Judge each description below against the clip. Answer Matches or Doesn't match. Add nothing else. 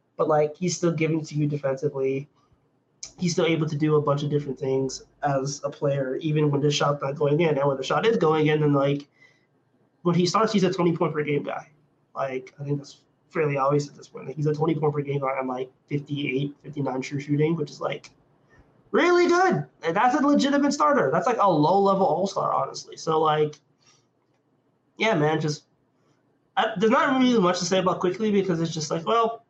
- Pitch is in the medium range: Matches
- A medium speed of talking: Doesn't match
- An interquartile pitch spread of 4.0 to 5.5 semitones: Doesn't match